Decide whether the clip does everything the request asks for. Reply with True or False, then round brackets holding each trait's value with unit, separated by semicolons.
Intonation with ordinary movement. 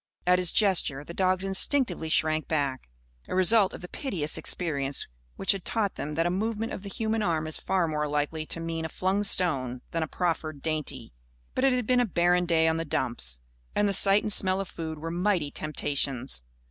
True (4.0 semitones)